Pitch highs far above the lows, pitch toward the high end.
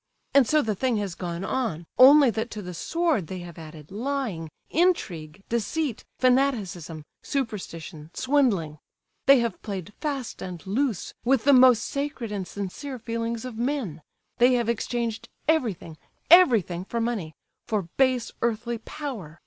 Yes: wide, 6.3 semitones; high, 230 Hz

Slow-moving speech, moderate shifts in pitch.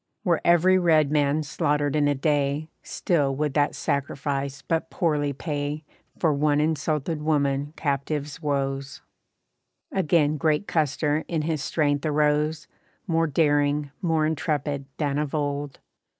No: slow, 130 wpm; narrow, 1.7 semitones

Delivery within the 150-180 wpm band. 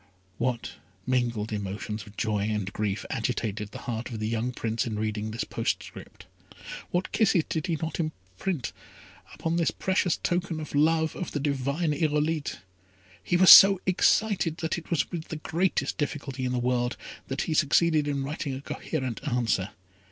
Yes: average, 170 wpm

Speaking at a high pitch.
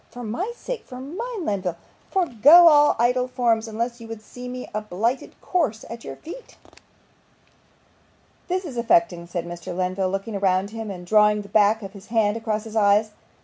Yes: high, 225 Hz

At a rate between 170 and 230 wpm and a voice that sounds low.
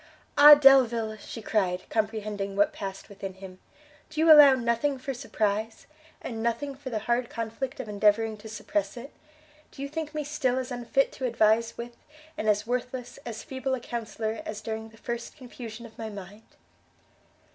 No: average, 175 wpm; high, 230 Hz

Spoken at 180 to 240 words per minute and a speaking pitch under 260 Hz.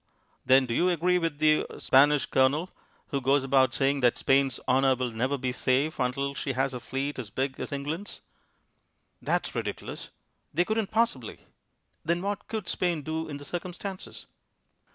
No: average, 170 wpm; medium, 140 Hz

